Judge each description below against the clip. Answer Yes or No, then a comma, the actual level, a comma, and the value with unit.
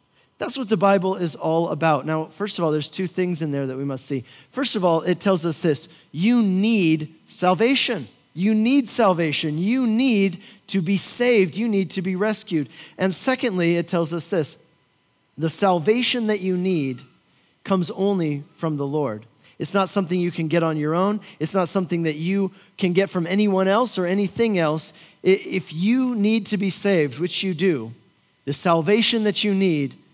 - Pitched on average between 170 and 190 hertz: Yes, medium, 185 Hz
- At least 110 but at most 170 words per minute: No, average, 190 wpm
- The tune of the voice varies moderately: Yes, average, 4.0 semitones